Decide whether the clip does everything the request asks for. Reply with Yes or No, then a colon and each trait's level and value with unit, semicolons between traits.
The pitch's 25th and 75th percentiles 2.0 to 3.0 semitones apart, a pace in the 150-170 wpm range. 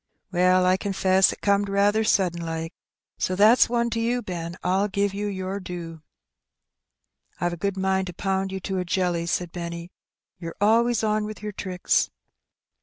No: narrow, 2.5 semitones; average, 185 wpm